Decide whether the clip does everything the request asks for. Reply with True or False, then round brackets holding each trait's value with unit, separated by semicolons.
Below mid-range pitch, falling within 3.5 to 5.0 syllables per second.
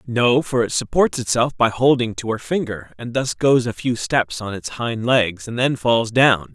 True (120 Hz; 4.4 syllables/s)